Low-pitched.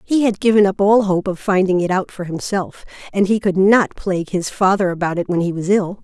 No: high, 190 Hz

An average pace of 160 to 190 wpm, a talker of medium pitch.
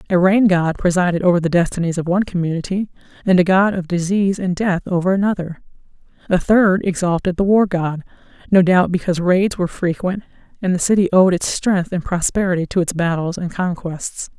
Yes: average, 185 wpm; medium, 180 Hz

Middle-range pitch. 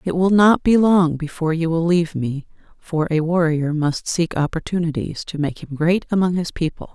Yes: medium, 165 Hz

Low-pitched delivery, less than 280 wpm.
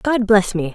No: high, 205 Hz; fast, 240 wpm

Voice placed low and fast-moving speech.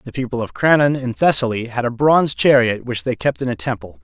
Yes: low, 125 Hz; fast, 240 wpm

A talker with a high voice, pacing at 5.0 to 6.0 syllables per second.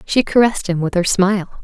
No: high, 195 Hz; 6.5 syllables/s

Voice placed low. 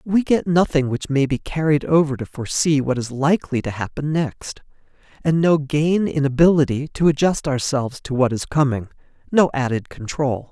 No: medium, 145 Hz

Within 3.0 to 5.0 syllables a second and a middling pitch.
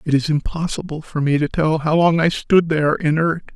No: 5.3 syllables/s; medium, 155 Hz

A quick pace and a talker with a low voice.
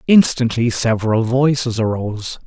No: slow, 95 wpm; low, 120 Hz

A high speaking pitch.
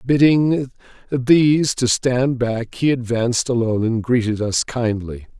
No: low, 125 Hz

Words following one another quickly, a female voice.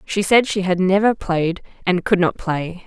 Yes: fast, 210 wpm; female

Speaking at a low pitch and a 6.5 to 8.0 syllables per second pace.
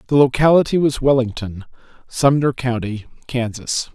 No: low, 125 Hz; 4.8 syllables/s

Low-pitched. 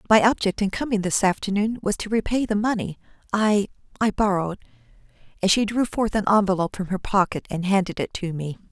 No: high, 200 Hz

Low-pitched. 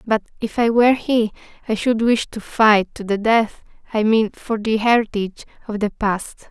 No: high, 220 Hz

